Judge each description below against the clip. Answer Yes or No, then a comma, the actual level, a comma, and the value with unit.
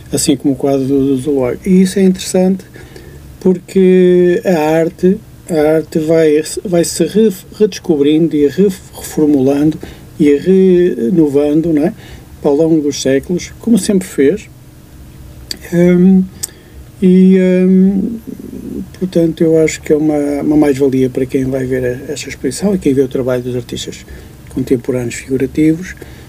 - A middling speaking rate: Yes, average, 130 wpm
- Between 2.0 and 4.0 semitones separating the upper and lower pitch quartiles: No, average, 5.1 semitones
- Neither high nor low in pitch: Yes, medium, 155 Hz